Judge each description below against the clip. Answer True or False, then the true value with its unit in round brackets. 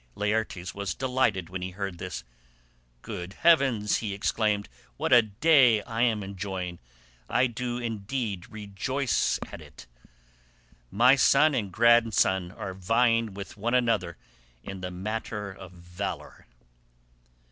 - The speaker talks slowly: True (125 wpm)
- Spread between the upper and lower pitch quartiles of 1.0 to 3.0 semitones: False (3.8 semitones)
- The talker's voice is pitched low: True (105 Hz)